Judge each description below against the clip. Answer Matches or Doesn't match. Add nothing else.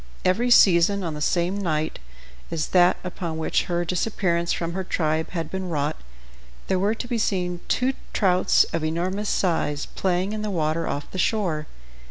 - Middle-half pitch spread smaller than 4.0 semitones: Matches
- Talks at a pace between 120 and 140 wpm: Doesn't match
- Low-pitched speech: Doesn't match